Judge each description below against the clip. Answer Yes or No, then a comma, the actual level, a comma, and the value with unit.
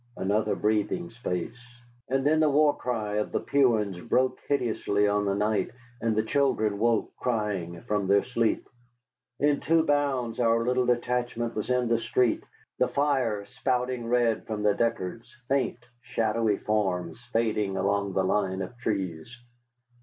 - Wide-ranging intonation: No, average, 3.3 semitones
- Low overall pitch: Yes, low, 115 Hz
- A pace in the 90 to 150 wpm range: Yes, average, 145 wpm